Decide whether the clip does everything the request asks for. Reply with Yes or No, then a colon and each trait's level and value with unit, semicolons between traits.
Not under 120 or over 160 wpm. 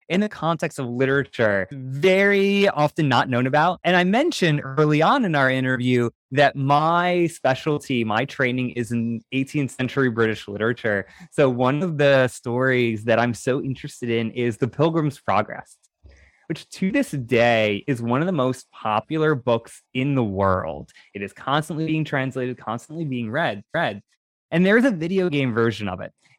No: average, 170 wpm